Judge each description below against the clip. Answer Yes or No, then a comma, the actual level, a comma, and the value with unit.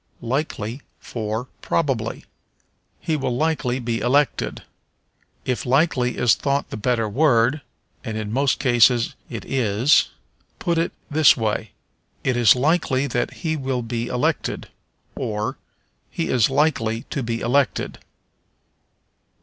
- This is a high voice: No, low, 125 Hz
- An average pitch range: Yes, average, 3.6 semitones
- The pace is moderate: No, slow, 125 wpm